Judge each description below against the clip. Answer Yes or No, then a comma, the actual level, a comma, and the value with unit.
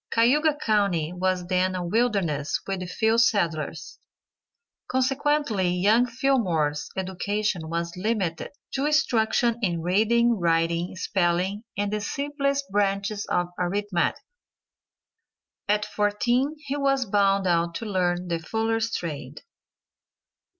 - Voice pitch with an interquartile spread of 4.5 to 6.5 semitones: Yes, average, 4.8 semitones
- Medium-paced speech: No, slow, 110 wpm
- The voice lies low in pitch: No, high, 200 Hz